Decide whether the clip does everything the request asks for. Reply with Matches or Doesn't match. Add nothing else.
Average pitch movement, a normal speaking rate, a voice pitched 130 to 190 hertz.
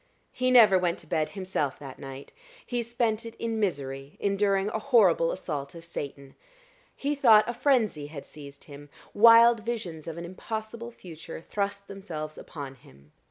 Doesn't match